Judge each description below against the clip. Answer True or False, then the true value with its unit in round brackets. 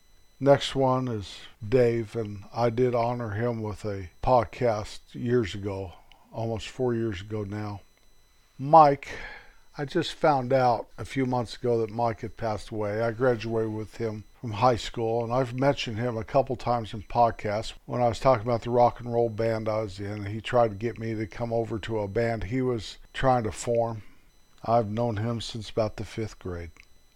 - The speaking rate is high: False (190 wpm)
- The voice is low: True (115 Hz)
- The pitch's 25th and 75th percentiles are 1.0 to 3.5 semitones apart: True (2.4 semitones)